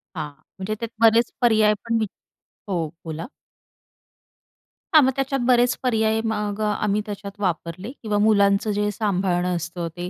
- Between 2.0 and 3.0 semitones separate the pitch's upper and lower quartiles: No, average, 3.4 semitones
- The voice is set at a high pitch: Yes, high, 210 Hz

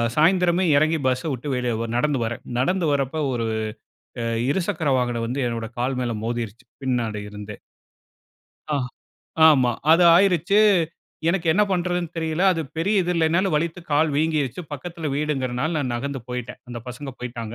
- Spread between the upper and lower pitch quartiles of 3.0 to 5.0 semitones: No, wide, 5.4 semitones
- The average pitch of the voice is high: No, medium, 145 Hz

